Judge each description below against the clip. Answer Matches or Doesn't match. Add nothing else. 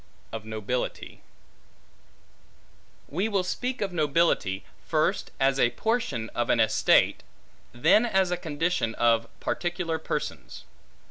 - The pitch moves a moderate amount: Doesn't match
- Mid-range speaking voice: Matches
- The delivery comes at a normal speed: Doesn't match